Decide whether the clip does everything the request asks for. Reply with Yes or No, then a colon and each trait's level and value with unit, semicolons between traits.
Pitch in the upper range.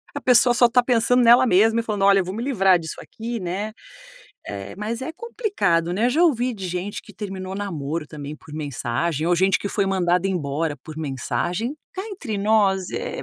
Yes: high, 195 Hz